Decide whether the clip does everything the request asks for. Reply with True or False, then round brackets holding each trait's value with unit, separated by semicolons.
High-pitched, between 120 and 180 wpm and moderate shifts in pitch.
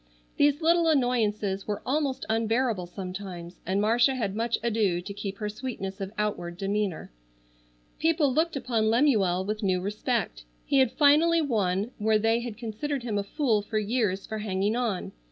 True (220 Hz; 165 wpm; 4.4 semitones)